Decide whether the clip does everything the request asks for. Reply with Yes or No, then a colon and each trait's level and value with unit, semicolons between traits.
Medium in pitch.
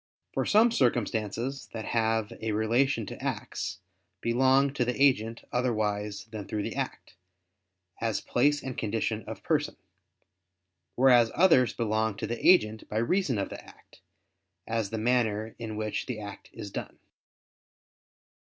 No: low, 115 Hz